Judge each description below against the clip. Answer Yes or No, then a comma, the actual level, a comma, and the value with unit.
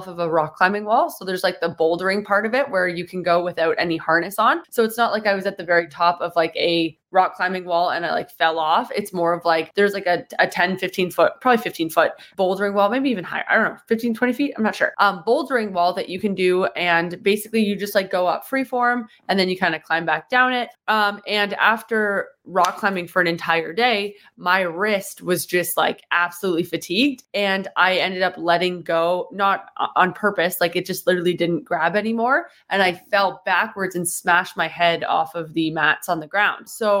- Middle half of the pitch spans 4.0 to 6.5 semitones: No, average, 3.1 semitones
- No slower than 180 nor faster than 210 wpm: No, fast, 230 wpm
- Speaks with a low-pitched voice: No, medium, 185 Hz